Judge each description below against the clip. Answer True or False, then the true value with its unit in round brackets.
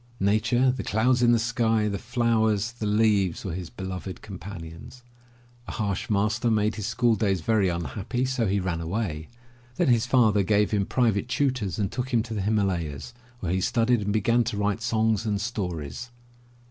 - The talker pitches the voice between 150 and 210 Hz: False (105 Hz)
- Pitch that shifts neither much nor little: True (3.3 semitones)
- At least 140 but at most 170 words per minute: False (185 wpm)